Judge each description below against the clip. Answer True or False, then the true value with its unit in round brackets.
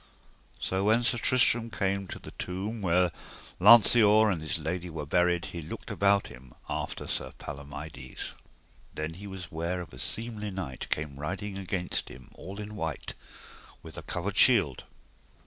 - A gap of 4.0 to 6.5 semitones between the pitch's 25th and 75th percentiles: True (4.6 semitones)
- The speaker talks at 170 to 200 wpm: False (160 wpm)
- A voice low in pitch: True (90 Hz)